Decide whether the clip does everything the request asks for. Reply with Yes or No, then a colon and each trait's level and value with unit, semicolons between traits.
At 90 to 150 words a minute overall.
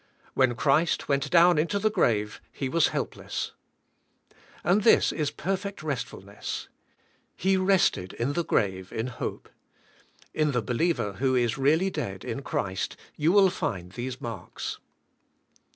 Yes: average, 140 wpm